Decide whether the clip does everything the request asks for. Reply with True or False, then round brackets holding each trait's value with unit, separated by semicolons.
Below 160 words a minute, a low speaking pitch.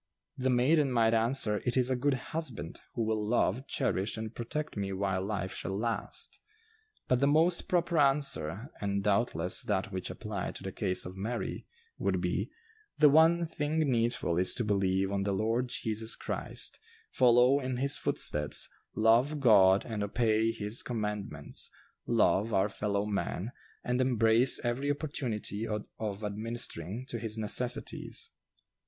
True (150 wpm; 115 Hz)